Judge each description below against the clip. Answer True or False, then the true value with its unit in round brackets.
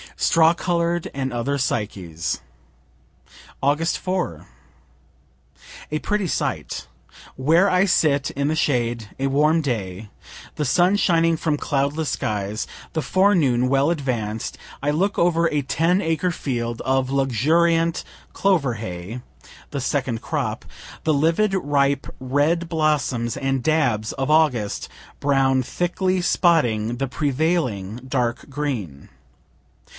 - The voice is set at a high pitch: False (140 Hz)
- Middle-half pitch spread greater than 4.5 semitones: True (5.1 semitones)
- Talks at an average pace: False (120 wpm)